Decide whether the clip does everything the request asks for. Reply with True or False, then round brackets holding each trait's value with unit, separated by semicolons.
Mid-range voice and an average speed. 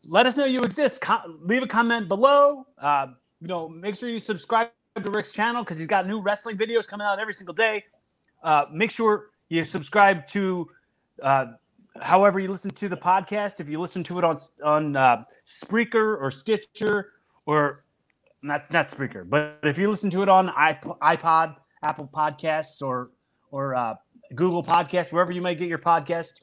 True (180 Hz; 185 wpm)